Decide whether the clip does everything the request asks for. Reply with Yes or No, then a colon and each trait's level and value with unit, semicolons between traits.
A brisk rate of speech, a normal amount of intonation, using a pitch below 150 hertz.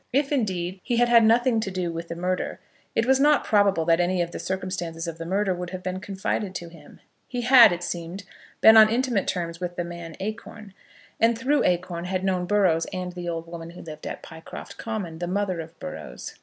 No: fast, 220 wpm; average, 4.1 semitones; medium, 185 Hz